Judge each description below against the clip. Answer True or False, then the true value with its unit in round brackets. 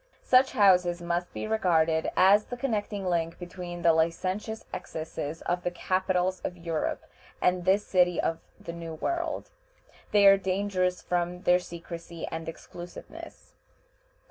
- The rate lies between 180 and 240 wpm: False (140 wpm)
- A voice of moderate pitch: True (180 Hz)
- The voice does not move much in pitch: True (2.2 semitones)